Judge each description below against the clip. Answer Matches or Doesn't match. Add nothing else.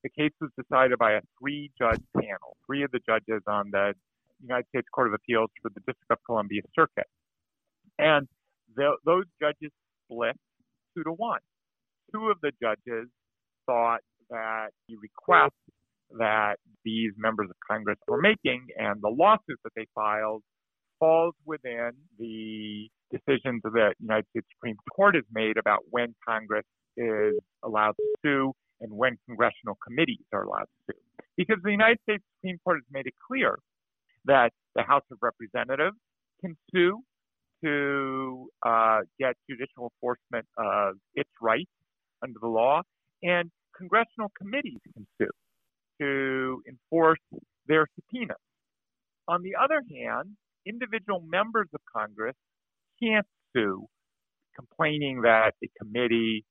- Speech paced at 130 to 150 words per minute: Matches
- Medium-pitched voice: Doesn't match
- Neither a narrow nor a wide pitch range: Doesn't match